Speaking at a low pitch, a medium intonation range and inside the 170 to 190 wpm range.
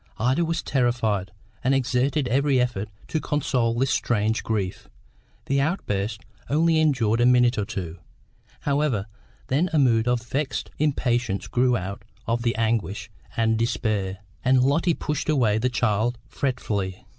No: low, 120 Hz; average, 4.0 semitones; average, 145 wpm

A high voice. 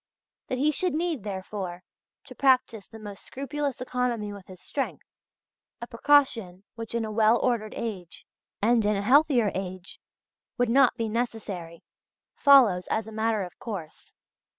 Yes: high, 225 Hz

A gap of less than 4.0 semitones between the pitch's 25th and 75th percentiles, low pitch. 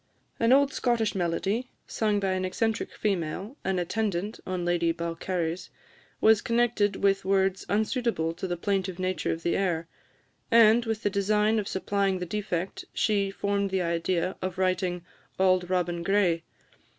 No: average, 3.0 semitones; high, 190 Hz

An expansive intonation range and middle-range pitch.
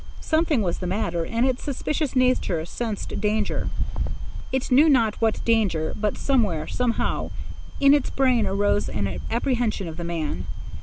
No: wide, 5.9 semitones; high, 225 Hz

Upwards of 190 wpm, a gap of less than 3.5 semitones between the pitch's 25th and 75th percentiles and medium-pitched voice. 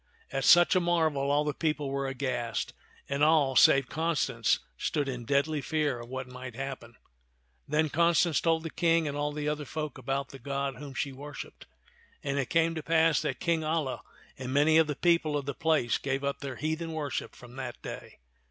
Yes: average, 200 wpm; average, 2.8 semitones; medium, 145 Hz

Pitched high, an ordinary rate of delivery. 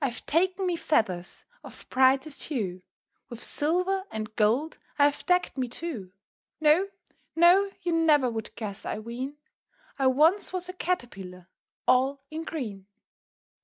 Yes: very high, 275 Hz; average, 145 wpm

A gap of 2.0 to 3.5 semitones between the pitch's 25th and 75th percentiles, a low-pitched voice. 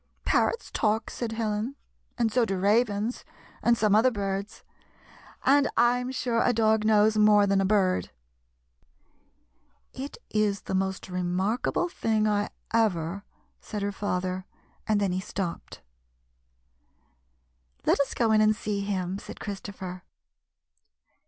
No: average, 2.7 semitones; high, 210 Hz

